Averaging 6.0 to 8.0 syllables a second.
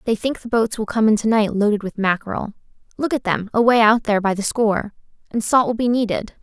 Yes: 6.1 syllables/s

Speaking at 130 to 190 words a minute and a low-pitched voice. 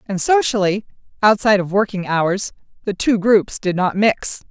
No: average, 160 wpm; high, 200 Hz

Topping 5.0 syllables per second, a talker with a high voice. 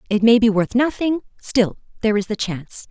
Yes: 5.6 syllables/s; high, 225 Hz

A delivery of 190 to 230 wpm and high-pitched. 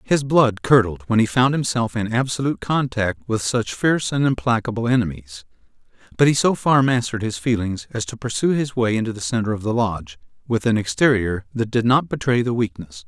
No: average, 195 wpm; low, 115 Hz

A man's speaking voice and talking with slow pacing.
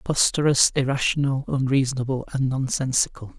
Yes: male; slow, 90 wpm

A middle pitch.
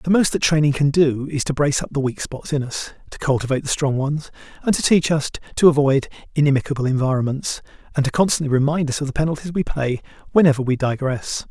Yes: medium, 145 Hz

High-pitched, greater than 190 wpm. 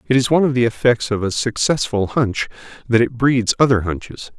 No: low, 120 Hz; fast, 205 wpm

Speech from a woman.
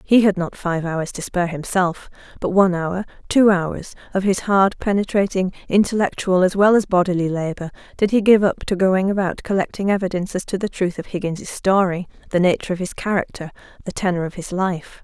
Yes: female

